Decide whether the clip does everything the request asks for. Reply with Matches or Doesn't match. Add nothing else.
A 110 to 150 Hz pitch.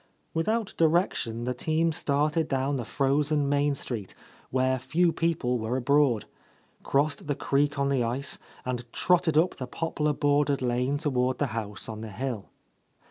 Matches